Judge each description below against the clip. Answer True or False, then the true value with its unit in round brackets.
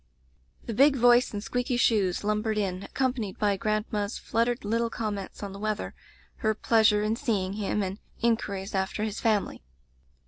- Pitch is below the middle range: False (215 Hz)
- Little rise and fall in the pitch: True (2.3 semitones)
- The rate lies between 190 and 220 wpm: False (170 wpm)